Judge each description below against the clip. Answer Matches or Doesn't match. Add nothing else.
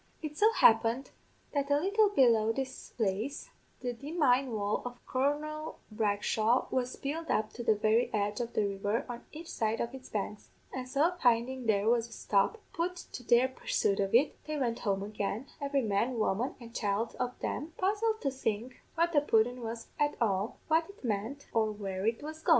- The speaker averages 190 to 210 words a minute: Matches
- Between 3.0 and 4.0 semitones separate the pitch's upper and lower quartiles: Doesn't match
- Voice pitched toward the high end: Matches